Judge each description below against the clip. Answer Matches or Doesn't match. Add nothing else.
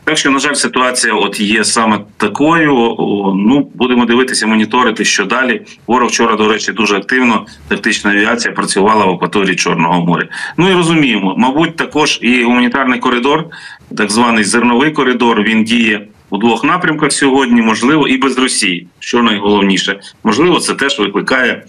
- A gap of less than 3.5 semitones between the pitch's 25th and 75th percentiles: Doesn't match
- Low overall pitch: Matches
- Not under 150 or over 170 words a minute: Matches